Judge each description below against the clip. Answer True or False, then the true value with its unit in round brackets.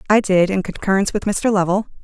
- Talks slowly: False (205 wpm)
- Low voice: False (195 Hz)